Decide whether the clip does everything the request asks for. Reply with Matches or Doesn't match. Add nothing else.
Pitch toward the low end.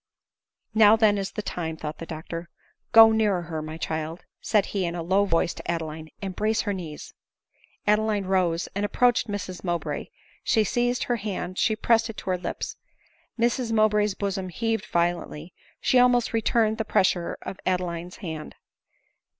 Doesn't match